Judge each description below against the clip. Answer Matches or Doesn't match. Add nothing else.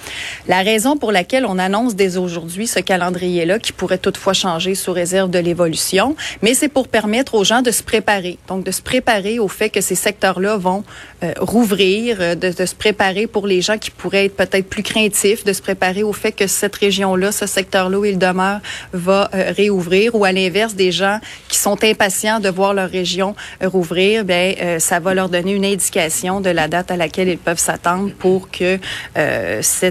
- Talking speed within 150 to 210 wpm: Matches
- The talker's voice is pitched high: Matches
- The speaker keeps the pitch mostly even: Matches